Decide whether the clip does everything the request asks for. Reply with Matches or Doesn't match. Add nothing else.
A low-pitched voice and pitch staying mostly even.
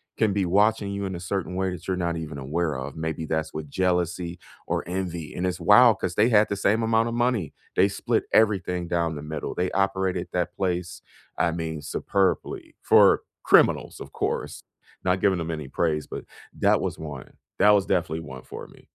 Doesn't match